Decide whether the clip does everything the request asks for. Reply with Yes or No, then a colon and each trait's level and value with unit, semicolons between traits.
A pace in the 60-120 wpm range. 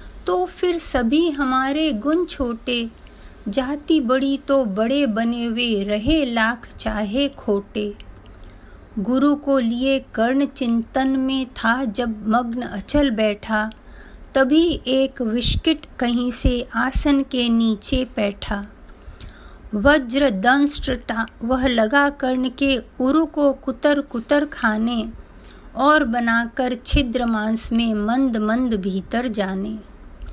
Yes: slow, 110 wpm